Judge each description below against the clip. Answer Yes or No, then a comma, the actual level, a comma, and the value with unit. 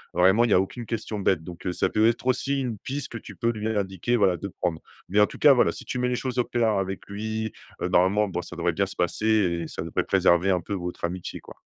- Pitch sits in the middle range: No, low, 100 Hz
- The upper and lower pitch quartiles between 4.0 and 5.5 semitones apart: Yes, average, 4.4 semitones